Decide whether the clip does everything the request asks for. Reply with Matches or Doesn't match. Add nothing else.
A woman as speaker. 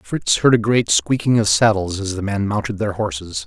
Doesn't match